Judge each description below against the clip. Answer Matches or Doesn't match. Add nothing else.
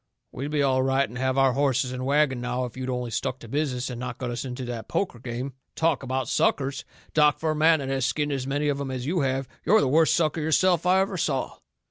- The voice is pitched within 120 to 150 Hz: Matches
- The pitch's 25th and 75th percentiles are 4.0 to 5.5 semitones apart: Doesn't match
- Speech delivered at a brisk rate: Matches